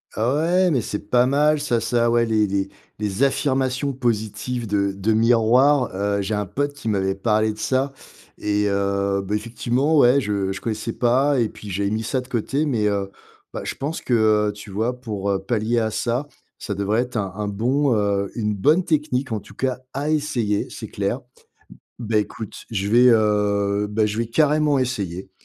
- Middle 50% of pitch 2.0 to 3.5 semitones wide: No, average, 3.9 semitones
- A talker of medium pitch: No, low, 110 Hz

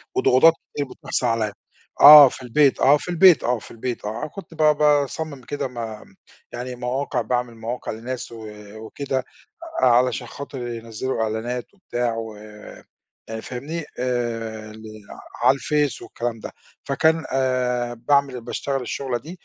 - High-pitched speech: No, low, 125 Hz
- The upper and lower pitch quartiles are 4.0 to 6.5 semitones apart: No, average, 3.5 semitones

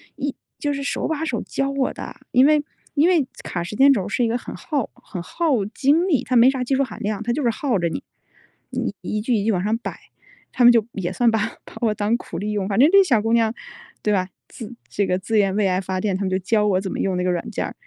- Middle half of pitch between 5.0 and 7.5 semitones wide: Yes, wide, 5.4 semitones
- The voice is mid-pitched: No, high, 225 Hz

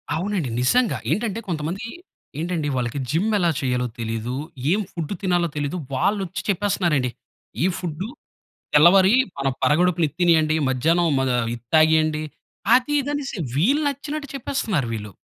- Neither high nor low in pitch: Yes, medium, 170 Hz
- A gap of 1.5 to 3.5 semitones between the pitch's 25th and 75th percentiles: No, wide, 5.6 semitones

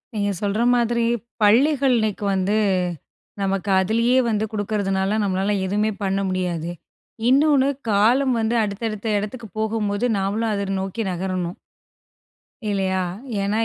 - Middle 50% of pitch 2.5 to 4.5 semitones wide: Yes, average, 2.8 semitones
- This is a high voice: Yes, high, 205 Hz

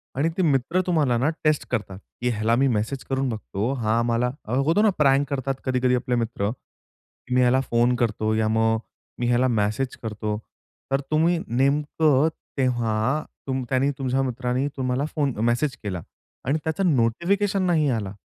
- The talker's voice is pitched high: No, low, 130 Hz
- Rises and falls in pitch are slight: No, average, 3.4 semitones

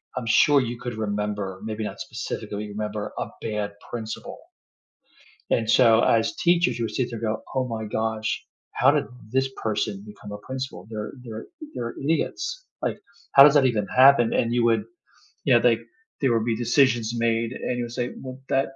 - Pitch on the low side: Yes, low, 115 Hz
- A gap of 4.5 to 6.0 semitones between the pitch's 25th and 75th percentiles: No, average, 2.9 semitones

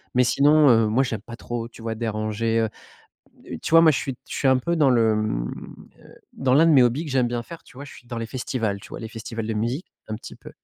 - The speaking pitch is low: Yes, low, 120 Hz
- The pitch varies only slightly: No, average, 3.2 semitones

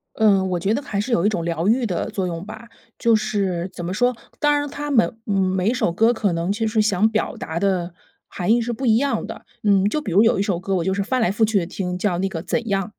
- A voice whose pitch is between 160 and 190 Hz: No, high, 205 Hz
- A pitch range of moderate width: Yes, average, 3.8 semitones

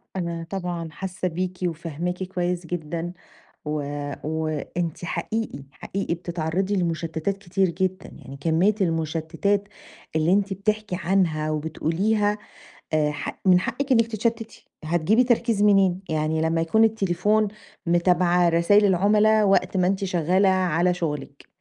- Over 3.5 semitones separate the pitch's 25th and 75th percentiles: No, average, 3.2 semitones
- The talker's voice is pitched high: No, medium, 180 Hz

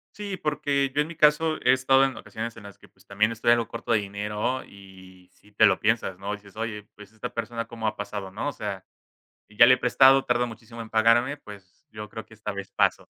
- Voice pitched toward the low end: Yes, low, 110 Hz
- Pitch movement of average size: Yes, average, 3.7 semitones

